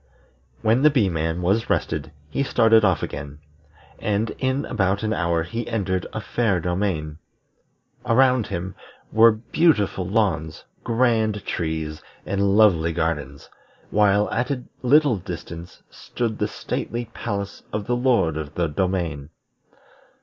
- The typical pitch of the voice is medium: No, low, 100 Hz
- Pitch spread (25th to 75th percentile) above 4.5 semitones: Yes, wide, 5.4 semitones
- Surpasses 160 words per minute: No, slow, 135 wpm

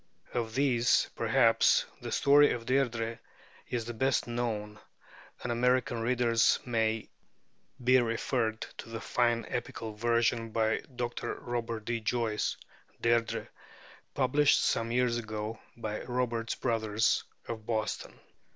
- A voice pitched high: No, low, 115 Hz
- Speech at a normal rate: No, slow, 120 wpm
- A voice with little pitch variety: Yes, narrow, 1.5 semitones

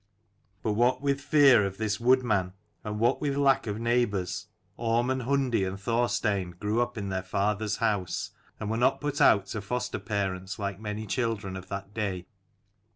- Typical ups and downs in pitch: Yes, average, 3.7 semitones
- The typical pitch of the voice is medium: No, low, 110 Hz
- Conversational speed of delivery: Yes, average, 180 wpm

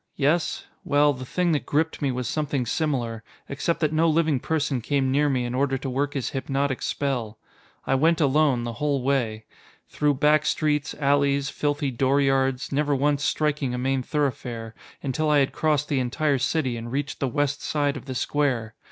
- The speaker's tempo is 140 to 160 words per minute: No, average, 185 wpm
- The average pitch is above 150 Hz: No, medium, 140 Hz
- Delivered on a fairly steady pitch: Yes, narrow, 2.2 semitones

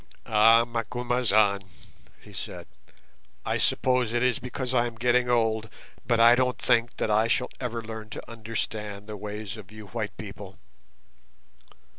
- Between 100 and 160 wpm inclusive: Yes, average, 150 wpm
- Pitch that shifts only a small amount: Yes, narrow, 2.2 semitones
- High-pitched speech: No, low, 115 Hz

